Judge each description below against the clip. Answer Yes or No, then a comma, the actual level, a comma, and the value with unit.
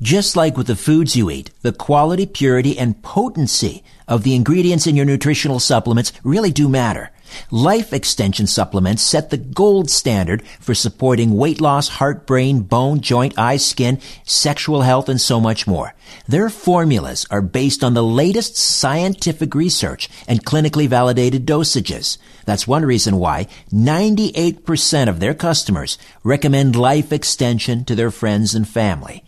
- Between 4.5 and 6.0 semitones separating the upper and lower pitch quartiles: Yes, average, 5.0 semitones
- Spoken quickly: No, average, 150 wpm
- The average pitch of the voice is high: No, low, 130 Hz